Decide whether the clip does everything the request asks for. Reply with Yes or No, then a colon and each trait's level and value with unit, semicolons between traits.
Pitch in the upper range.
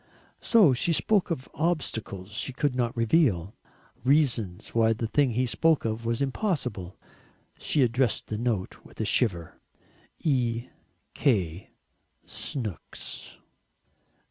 No: low, 120 Hz